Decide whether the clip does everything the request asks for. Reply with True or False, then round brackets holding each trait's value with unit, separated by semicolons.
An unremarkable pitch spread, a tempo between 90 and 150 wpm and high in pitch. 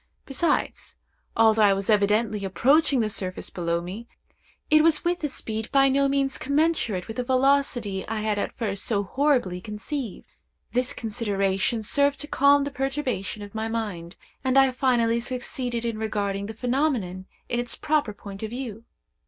False (4.9 semitones; 165 wpm; 230 Hz)